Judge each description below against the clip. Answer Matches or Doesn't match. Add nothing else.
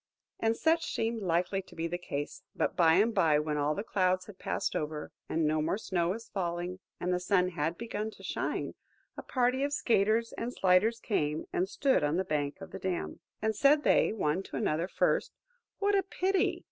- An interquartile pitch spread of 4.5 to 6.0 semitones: Matches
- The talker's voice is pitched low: Doesn't match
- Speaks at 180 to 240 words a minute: Matches